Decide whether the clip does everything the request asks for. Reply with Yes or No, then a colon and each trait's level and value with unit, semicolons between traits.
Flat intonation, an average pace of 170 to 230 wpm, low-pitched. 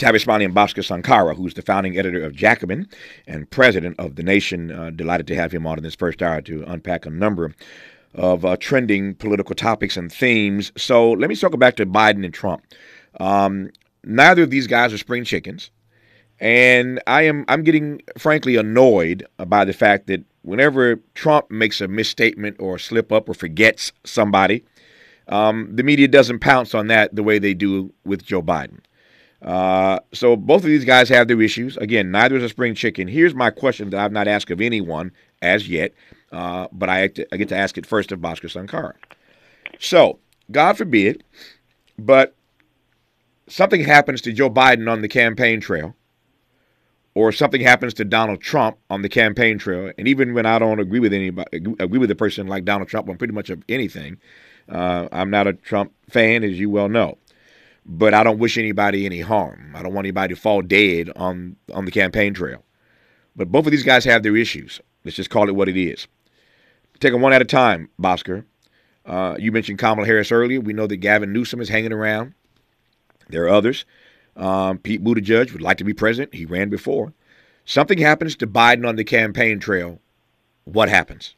No: average, 3.7 semitones; average, 195 wpm; low, 105 Hz